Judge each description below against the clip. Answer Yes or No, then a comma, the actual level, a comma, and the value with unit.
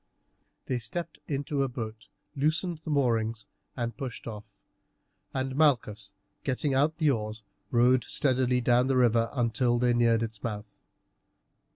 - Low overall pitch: Yes, low, 125 Hz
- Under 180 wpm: Yes, average, 140 wpm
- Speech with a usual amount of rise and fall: Yes, average, 3.2 semitones